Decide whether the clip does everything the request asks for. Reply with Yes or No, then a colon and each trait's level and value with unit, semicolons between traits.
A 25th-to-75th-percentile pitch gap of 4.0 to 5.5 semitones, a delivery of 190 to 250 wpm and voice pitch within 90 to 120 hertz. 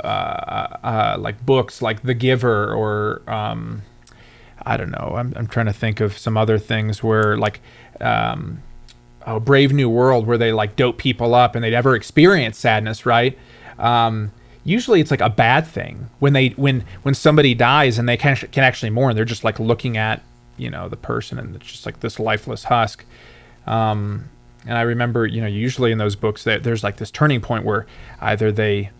No: average, 2.7 semitones; average, 200 wpm; low, 115 Hz